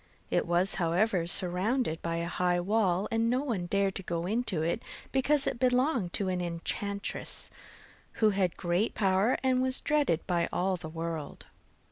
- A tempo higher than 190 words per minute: No, average, 165 wpm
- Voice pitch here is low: No, high, 190 Hz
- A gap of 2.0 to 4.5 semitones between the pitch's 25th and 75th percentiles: No, average, 5.0 semitones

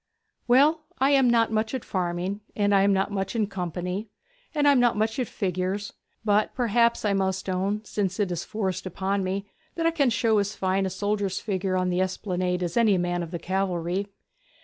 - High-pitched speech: Yes, high, 200 Hz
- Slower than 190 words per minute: No, fast, 205 wpm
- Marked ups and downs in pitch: No, average, 3.0 semitones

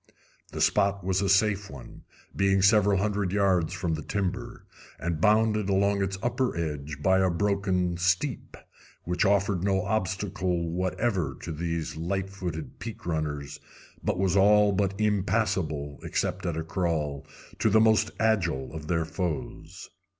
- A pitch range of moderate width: Yes, average, 3.4 semitones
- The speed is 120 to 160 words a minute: Yes, average, 150 wpm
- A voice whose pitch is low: Yes, very low, 95 Hz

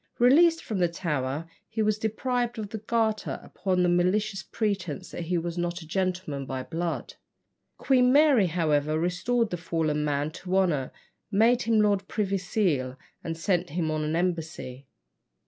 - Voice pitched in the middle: Yes, medium, 180 Hz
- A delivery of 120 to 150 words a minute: No, average, 165 wpm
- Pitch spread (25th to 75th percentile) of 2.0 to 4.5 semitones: No, average, 5.0 semitones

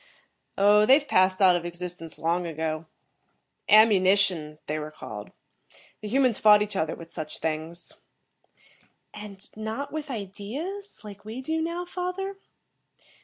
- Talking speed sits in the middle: No, slow, 130 wpm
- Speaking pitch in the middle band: No, high, 200 Hz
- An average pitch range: No, wide, 7.3 semitones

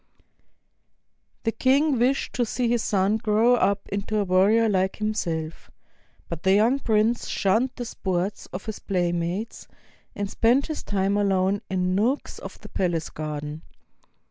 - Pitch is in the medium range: No, high, 205 Hz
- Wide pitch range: No, average, 3.7 semitones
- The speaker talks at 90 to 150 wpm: Yes, average, 145 wpm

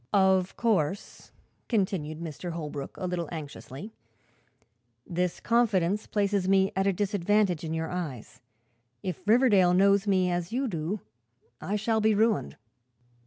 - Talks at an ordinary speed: No, slow, 125 wpm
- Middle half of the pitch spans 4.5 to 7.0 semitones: No, average, 3.6 semitones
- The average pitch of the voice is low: No, high, 190 Hz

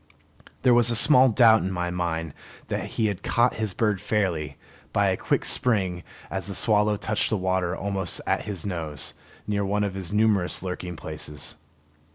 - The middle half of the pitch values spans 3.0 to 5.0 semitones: Yes, average, 3.3 semitones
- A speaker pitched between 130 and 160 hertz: No, very low, 95 Hz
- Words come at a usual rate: Yes, average, 175 wpm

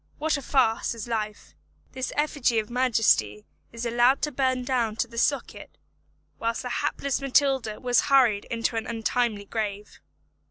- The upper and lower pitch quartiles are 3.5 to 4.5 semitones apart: No, average, 2.8 semitones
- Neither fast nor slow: Yes, average, 155 wpm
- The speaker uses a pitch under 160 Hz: No, high, 240 Hz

